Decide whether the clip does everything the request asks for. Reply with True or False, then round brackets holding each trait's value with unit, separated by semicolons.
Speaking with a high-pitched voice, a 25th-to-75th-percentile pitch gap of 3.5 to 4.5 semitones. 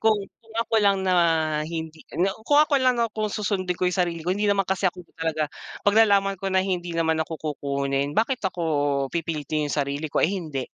False (180 Hz; 4.1 semitones)